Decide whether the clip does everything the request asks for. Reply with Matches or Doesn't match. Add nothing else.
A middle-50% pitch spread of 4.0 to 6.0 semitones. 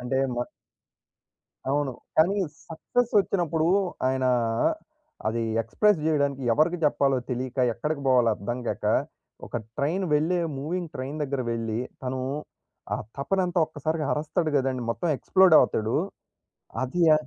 Matches